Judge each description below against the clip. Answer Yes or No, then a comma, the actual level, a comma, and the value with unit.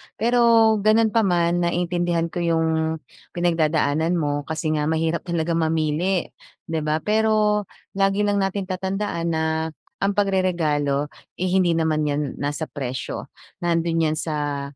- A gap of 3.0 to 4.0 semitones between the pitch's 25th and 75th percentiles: Yes, average, 3.5 semitones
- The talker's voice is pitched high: No, medium, 170 Hz